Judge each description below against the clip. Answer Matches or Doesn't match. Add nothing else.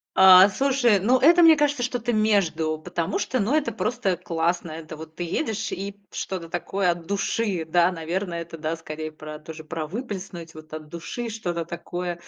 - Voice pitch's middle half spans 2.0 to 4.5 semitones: Doesn't match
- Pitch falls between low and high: Matches